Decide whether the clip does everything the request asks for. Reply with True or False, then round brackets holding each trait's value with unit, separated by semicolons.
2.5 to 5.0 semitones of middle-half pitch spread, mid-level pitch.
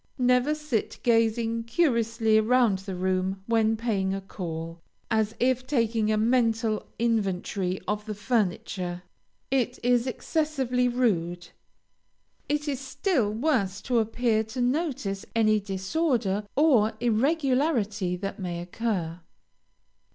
False (4.2 semitones; 225 Hz)